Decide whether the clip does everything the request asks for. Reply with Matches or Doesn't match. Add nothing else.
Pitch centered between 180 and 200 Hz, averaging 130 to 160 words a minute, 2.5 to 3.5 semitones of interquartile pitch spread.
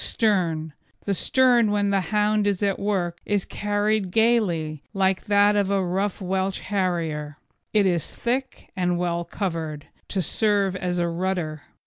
Matches